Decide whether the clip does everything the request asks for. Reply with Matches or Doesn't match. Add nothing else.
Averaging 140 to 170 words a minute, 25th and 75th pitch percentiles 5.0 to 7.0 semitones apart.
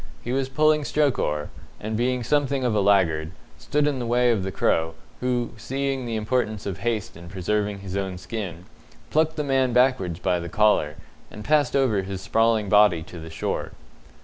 Doesn't match